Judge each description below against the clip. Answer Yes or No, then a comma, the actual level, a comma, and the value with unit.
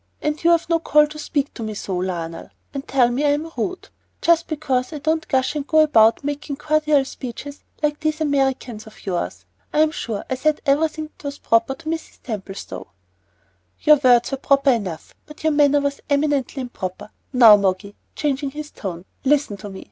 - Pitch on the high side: Yes, very high, 280 Hz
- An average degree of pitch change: Yes, average, 4.9 semitones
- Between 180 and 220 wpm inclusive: Yes, average, 185 wpm